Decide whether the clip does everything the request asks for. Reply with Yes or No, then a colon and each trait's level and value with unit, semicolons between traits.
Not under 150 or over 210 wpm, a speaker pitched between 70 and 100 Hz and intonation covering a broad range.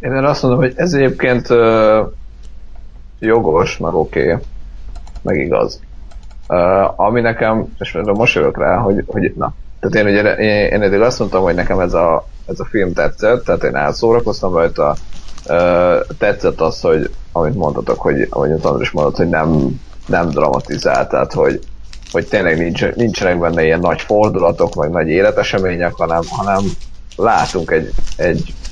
Yes: fast, 155 wpm; very low, 95 Hz; wide, 6.3 semitones